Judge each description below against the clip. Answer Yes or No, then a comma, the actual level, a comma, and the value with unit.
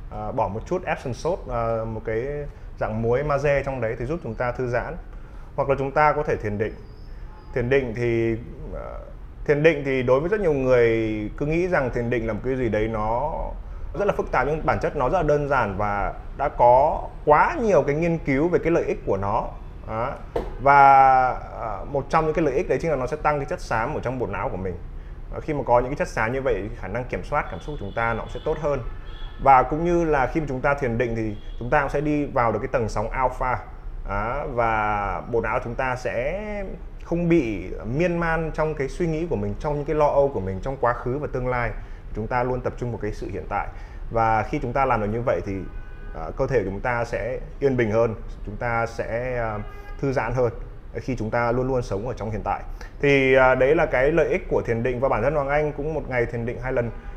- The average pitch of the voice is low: Yes, low, 125 Hz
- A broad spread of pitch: No, average, 4.5 semitones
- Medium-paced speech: No, fast, 255 wpm